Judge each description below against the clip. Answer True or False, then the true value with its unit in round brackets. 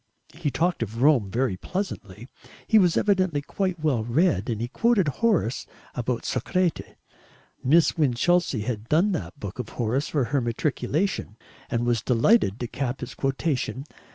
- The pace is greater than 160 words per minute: False (155 wpm)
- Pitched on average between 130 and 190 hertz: True (135 Hz)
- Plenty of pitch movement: True (6.6 semitones)